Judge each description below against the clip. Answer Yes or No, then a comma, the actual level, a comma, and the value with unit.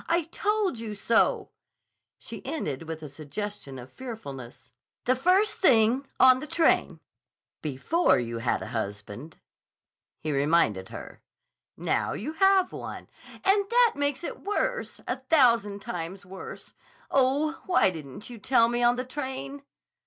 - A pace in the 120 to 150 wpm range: Yes, average, 140 wpm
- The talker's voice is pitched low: No, high, 240 Hz